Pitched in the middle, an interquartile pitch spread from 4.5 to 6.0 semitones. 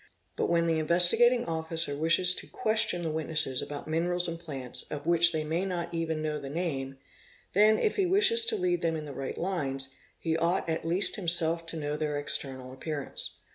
No: medium, 165 Hz; average, 2.8 semitones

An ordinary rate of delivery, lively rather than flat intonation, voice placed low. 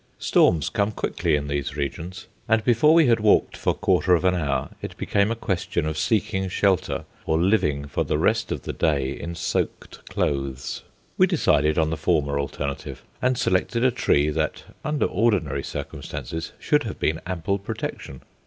Yes: average, 170 wpm; wide, 5.8 semitones; very low, 85 Hz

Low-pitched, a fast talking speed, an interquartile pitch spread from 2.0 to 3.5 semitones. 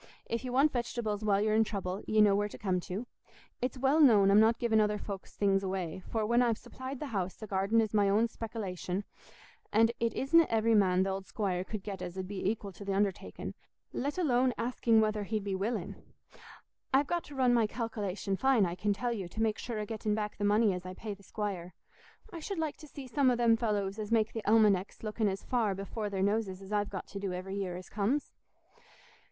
No: high, 210 Hz; fast, 225 wpm; average, 2.9 semitones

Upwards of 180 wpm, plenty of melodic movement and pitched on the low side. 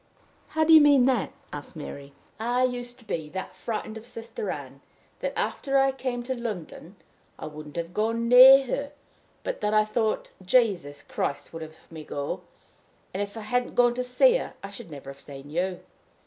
No: average, 190 wpm; wide, 7.3 semitones; high, 220 Hz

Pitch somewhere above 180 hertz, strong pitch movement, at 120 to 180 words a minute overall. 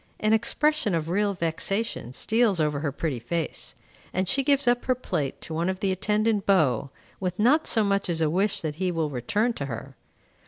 No: high, 190 Hz; wide, 5.7 semitones; average, 200 wpm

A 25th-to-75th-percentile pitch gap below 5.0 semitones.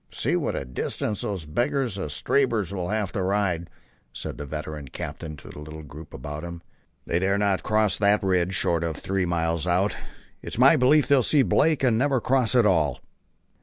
No: average, 5.3 semitones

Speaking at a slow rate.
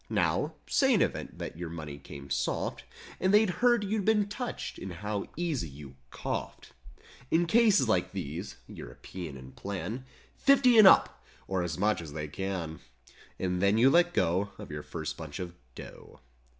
No: average, 170 wpm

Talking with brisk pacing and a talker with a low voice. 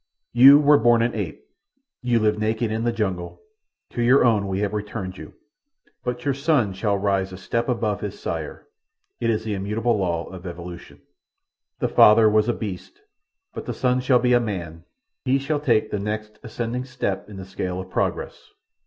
No: average, 180 wpm; low, 110 Hz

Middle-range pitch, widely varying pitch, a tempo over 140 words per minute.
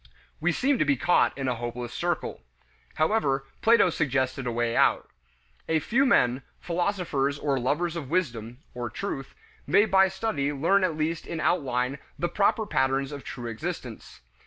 Yes: medium, 145 Hz; wide, 5.8 semitones; average, 160 wpm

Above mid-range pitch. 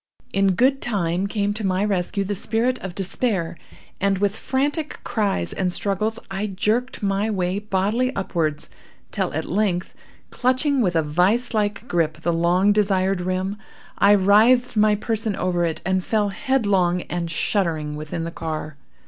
Yes: high, 195 Hz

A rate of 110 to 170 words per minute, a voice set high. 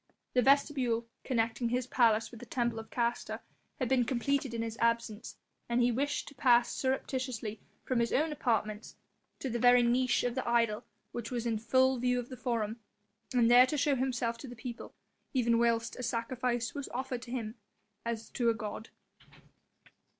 No: average, 180 wpm; high, 240 Hz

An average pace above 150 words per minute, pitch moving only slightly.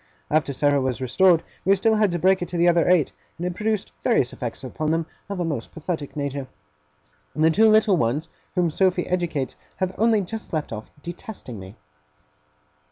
No: average, 190 wpm; average, 4.8 semitones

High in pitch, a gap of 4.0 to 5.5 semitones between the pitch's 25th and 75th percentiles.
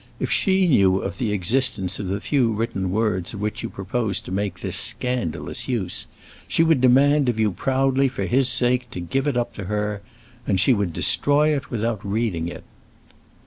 No: low, 115 Hz; average, 4.8 semitones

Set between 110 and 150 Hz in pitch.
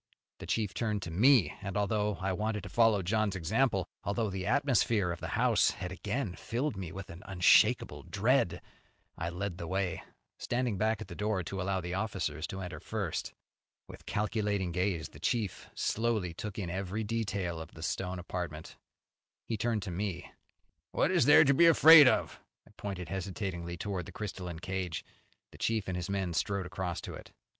No: very low, 95 Hz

